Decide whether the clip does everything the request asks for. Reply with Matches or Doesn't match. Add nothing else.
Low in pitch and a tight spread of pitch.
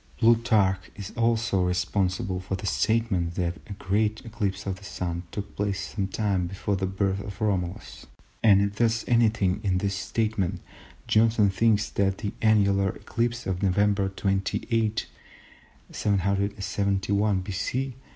Matches